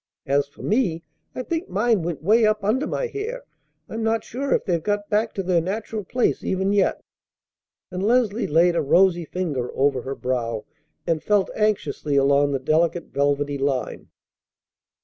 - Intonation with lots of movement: Yes, wide, 7.1 semitones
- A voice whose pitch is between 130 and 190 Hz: Yes, medium, 185 Hz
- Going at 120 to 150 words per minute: No, average, 170 wpm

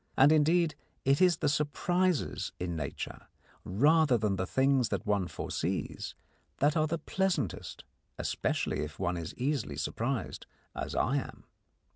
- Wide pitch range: Yes, wide, 8.2 semitones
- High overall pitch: No, medium, 140 Hz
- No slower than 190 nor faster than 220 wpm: No, average, 140 wpm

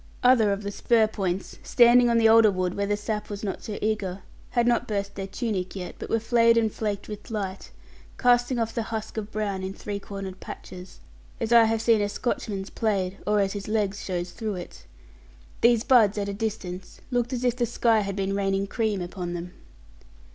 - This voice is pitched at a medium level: No, high, 210 Hz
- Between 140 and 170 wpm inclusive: No, fast, 205 wpm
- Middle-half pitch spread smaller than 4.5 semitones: Yes, narrow, 2.6 semitones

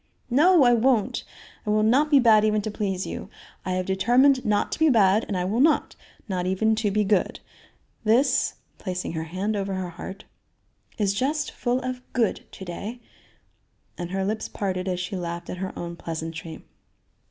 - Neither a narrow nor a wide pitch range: Yes, average, 4.5 semitones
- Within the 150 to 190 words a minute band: Yes, average, 185 wpm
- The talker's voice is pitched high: Yes, high, 205 Hz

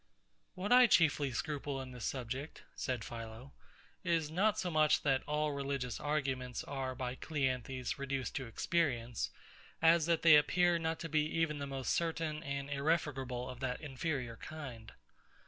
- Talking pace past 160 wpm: No, average, 155 wpm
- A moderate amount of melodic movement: Yes, average, 3.7 semitones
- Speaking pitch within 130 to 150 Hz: Yes, medium, 140 Hz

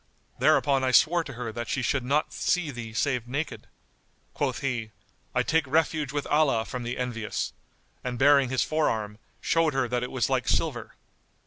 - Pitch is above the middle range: No, low, 130 Hz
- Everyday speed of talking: Yes, average, 180 wpm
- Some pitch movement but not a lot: Yes, average, 3.3 semitones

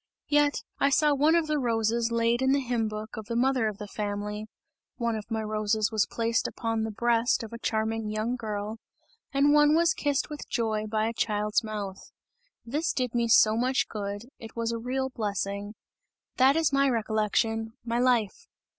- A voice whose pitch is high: Yes, high, 230 Hz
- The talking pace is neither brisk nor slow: Yes, average, 190 wpm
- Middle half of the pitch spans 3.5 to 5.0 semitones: No, average, 3.0 semitones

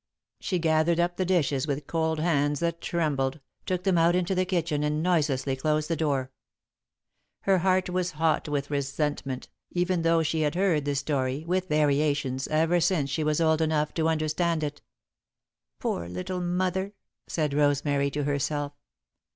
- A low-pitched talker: No, medium, 155 Hz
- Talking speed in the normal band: Yes, average, 160 wpm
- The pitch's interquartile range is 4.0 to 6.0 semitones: No, average, 3.2 semitones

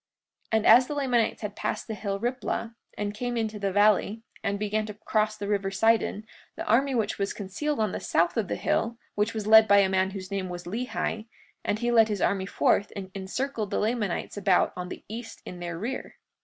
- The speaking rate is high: Yes, fast, 220 wpm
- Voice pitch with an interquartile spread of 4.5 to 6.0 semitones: No, narrow, 2.4 semitones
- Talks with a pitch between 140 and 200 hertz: No, high, 210 Hz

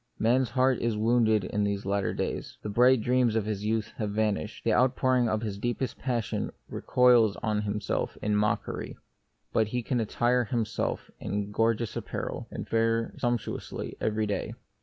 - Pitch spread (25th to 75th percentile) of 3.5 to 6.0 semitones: No, narrow, 2.4 semitones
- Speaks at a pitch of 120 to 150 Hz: No, low, 110 Hz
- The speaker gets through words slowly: No, average, 165 wpm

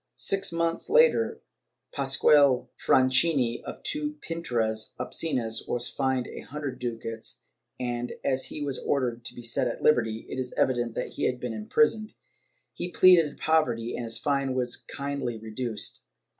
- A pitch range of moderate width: Yes, average, 4.0 semitones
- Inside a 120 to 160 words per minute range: Yes, average, 150 wpm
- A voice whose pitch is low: Yes, low, 130 Hz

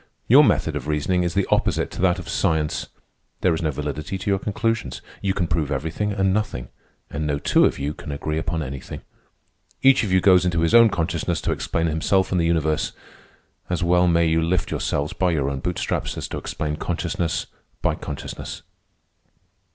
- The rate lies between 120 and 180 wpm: No, average, 190 wpm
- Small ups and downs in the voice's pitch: No, average, 3.5 semitones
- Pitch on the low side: Yes, very low, 85 Hz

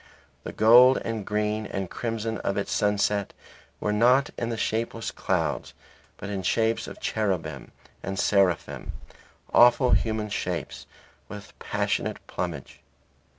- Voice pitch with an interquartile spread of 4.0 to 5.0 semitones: No, narrow, 2.5 semitones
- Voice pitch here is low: Yes, low, 105 Hz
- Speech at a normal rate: No, slow, 130 wpm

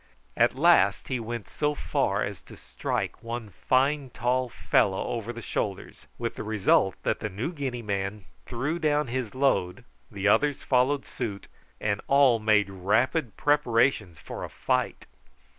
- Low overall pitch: Yes, low, 120 Hz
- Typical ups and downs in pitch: Yes, average, 4.7 semitones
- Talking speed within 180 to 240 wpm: No, average, 155 wpm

